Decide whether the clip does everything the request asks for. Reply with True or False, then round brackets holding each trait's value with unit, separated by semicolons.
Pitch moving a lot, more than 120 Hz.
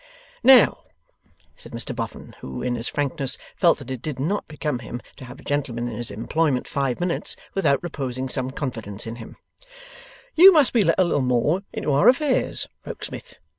True (5.8 semitones; 140 Hz)